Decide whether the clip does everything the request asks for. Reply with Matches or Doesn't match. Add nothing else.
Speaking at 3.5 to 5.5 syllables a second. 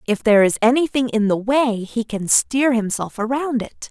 Matches